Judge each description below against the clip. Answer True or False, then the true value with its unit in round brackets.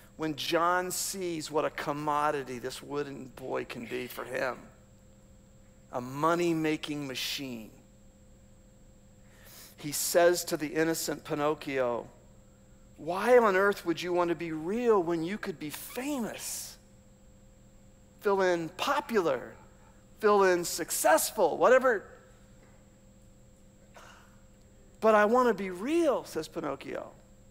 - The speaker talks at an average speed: False (115 wpm)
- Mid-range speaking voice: True (160 Hz)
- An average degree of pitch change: False (5.8 semitones)